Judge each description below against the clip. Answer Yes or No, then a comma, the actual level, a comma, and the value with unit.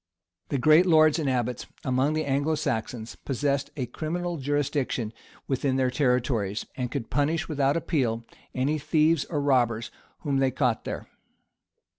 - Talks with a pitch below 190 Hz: Yes, low, 135 Hz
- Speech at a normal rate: Yes, average, 150 wpm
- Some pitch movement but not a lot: Yes, average, 3.5 semitones